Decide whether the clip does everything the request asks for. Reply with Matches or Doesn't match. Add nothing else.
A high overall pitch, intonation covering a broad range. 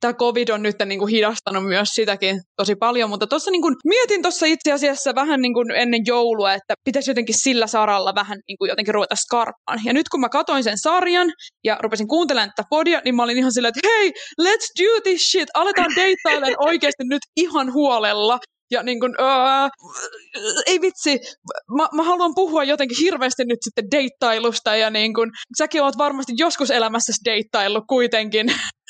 Matches